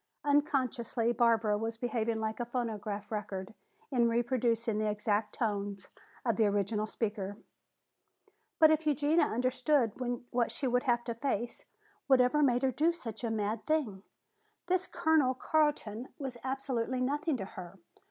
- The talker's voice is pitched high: Yes, high, 235 Hz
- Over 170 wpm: No, average, 145 wpm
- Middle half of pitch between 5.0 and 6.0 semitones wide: No, average, 3.8 semitones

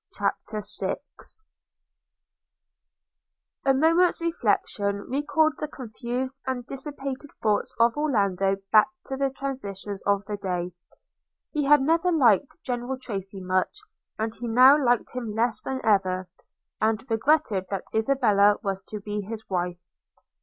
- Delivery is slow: Yes, slow, 130 wpm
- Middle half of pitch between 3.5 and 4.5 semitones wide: No, average, 5.2 semitones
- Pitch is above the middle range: Yes, high, 230 Hz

